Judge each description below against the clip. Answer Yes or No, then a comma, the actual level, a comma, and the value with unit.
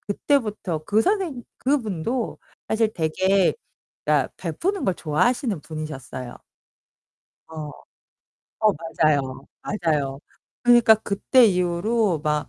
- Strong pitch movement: Yes, wide, 6.8 semitones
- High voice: Yes, high, 195 Hz